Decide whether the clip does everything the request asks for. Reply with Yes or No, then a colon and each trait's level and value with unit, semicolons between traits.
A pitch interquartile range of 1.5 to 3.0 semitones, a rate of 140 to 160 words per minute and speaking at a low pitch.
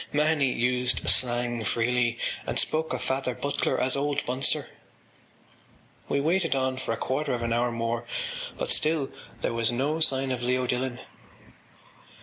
Yes: average, 2.7 semitones; average, 150 wpm; low, 130 Hz